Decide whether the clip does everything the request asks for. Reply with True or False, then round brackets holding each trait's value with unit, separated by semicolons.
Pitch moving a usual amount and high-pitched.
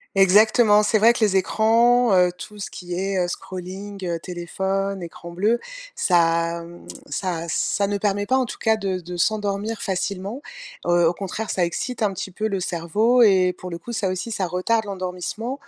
True (3.3 semitones; 195 Hz)